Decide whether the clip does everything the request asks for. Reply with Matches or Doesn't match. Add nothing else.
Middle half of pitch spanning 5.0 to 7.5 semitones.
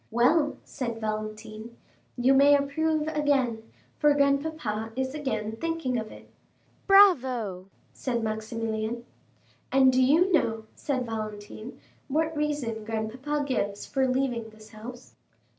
Doesn't match